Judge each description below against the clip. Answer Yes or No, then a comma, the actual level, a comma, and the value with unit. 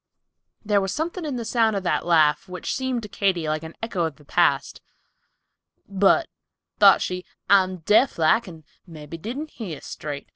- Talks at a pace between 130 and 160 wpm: No, average, 175 wpm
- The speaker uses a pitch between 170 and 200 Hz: Yes, medium, 185 Hz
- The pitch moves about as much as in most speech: No, wide, 5.9 semitones